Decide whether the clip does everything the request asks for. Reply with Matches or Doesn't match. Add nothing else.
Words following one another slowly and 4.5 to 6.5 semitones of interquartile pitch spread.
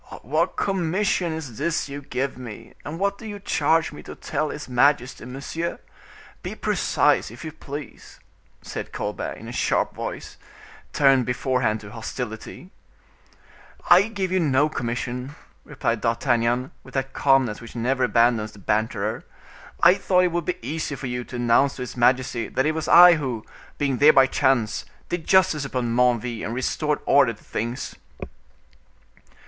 Doesn't match